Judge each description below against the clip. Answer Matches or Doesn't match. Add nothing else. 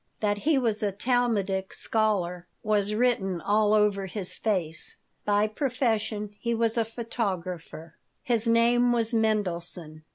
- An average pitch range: Matches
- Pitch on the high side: Matches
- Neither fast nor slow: Doesn't match